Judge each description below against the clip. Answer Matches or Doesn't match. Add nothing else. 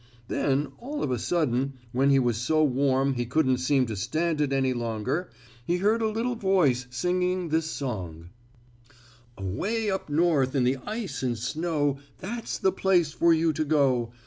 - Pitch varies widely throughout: Matches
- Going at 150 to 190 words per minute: Matches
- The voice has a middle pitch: Matches